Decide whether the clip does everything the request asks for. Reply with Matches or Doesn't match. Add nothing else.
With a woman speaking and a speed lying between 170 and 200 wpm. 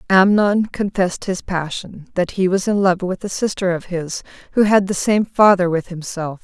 Matches